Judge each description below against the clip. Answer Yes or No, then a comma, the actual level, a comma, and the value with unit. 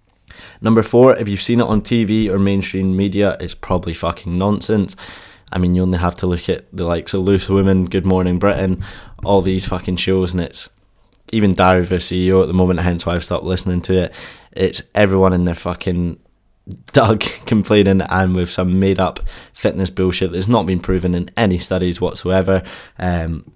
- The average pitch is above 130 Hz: No, very low, 95 Hz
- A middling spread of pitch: No, narrow, 1.6 semitones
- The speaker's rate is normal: Yes, average, 190 wpm